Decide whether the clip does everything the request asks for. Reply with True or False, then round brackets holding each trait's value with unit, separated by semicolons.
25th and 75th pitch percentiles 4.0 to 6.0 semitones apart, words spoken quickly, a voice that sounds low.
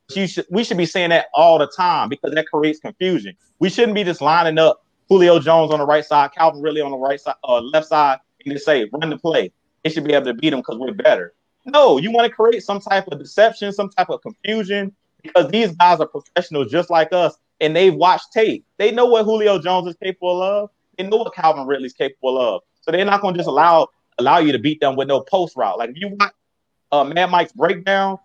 False (4.7 semitones; 245 wpm; 175 Hz)